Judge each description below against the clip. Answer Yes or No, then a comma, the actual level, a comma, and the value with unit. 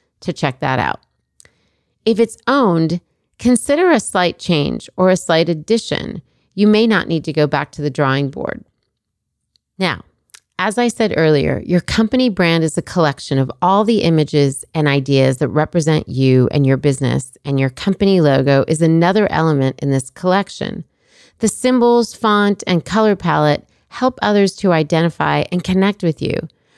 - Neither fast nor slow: Yes, average, 165 wpm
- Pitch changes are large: Yes, wide, 5.7 semitones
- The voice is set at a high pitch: No, medium, 165 Hz